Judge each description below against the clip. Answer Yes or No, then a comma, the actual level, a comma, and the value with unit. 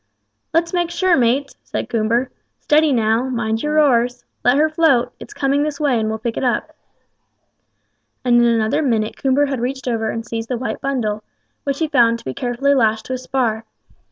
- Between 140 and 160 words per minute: No, average, 195 wpm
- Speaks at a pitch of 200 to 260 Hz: Yes, very high, 250 Hz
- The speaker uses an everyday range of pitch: Yes, average, 3.6 semitones